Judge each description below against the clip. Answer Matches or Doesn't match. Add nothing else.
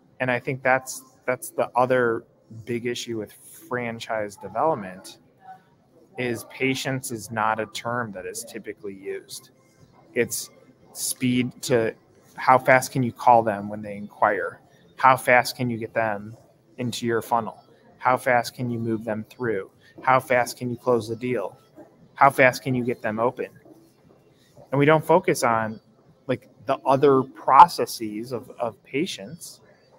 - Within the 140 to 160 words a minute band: Matches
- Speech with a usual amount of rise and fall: Doesn't match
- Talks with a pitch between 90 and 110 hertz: Doesn't match